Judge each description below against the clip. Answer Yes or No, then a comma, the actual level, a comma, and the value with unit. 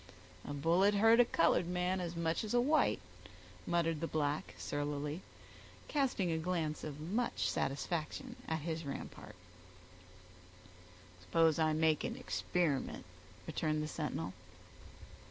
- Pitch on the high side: No, medium, 165 Hz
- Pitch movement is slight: No, average, 3.0 semitones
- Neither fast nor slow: No, slow, 125 wpm